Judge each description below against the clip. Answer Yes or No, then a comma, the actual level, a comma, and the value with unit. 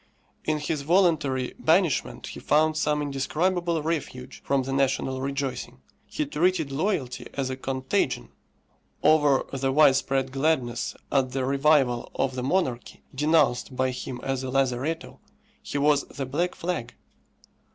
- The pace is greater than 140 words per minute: No, slow, 135 wpm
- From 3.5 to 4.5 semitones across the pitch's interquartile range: No, average, 3.0 semitones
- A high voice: No, medium, 140 Hz